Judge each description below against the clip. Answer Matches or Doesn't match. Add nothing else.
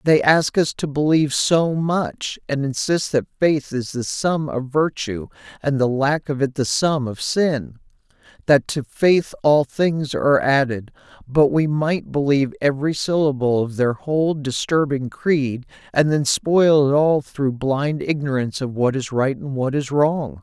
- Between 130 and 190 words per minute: Matches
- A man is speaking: Matches